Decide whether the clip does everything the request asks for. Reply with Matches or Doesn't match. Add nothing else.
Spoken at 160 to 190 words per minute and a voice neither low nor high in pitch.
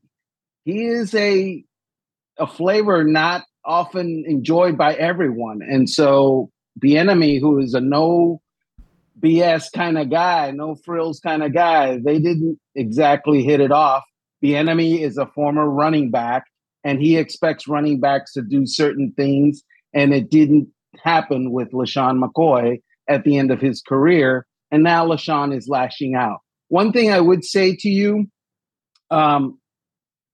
Doesn't match